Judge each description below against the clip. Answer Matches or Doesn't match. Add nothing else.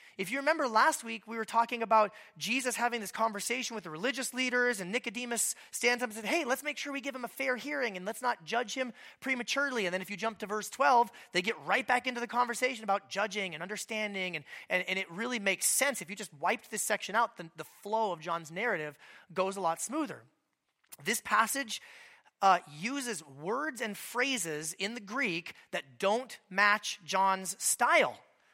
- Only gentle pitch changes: Doesn't match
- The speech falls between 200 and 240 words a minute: Matches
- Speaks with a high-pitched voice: Matches